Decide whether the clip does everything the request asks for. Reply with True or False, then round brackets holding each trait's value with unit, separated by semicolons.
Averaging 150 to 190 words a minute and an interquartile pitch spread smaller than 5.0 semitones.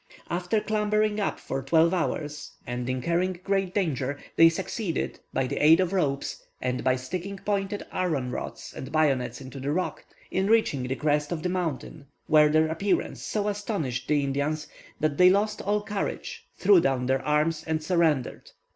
False (170 wpm; 5.4 semitones)